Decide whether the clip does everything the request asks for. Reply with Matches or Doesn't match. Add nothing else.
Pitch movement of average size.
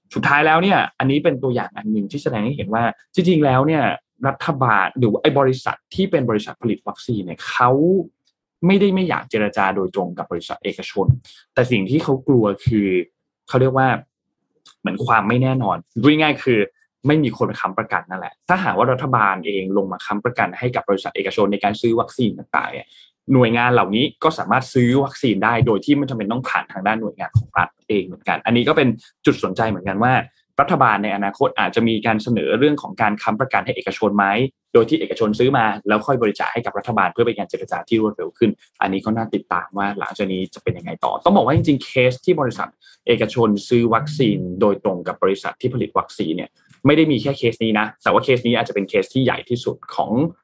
Matches